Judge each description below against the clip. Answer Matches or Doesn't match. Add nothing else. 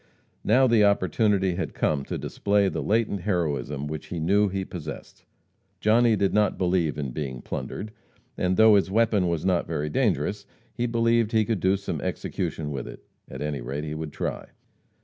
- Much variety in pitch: Matches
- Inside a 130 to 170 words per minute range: Doesn't match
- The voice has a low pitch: Matches